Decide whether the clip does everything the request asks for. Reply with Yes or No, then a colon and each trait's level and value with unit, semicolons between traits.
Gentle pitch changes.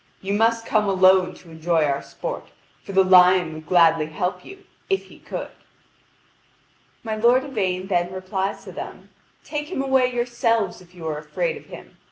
No: average, 5.2 semitones